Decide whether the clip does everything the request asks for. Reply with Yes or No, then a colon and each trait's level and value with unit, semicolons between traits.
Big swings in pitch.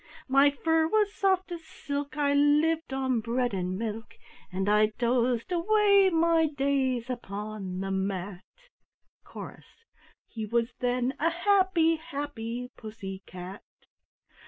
Yes: wide, 7.0 semitones